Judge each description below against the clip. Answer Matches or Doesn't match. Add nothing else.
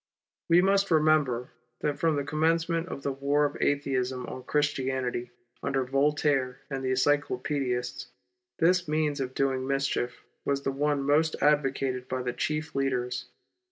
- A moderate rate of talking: Matches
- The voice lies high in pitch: Doesn't match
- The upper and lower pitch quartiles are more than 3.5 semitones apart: Doesn't match